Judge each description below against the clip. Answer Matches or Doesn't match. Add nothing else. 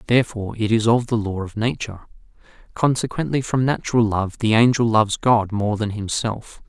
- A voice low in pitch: Matches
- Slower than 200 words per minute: Matches